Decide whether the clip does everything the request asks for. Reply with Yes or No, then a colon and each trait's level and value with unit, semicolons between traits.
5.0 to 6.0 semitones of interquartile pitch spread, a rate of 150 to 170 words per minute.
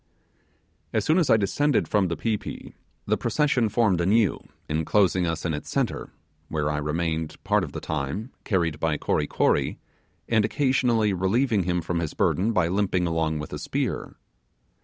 Yes: average, 5.3 semitones; average, 165 wpm